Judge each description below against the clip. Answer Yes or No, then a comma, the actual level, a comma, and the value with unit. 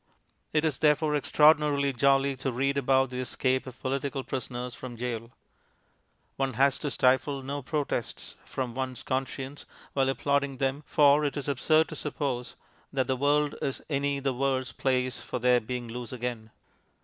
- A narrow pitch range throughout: Yes, narrow, 2.0 semitones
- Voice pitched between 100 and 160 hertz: Yes, low, 135 Hz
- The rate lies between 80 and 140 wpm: No, average, 160 wpm